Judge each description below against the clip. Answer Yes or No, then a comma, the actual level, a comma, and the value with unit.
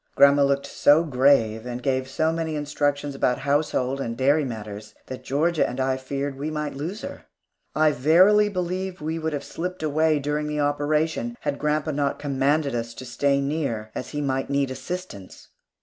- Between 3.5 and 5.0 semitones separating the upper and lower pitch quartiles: No, average, 2.9 semitones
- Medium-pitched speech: Yes, medium, 145 Hz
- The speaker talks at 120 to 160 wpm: No, average, 180 wpm